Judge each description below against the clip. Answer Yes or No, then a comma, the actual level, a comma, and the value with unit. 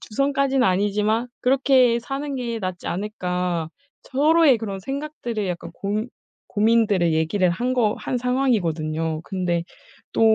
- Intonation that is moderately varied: No, wide, 5.9 semitones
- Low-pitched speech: No, high, 215 Hz